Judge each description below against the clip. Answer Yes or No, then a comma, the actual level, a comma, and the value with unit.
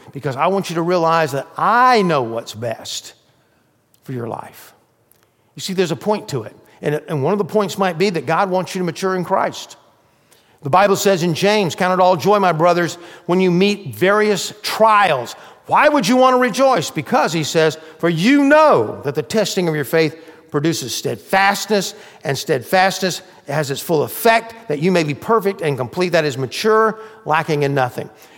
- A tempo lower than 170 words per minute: No, average, 195 wpm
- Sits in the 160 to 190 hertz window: Yes, medium, 185 Hz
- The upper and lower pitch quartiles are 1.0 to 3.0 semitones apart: No, average, 4.7 semitones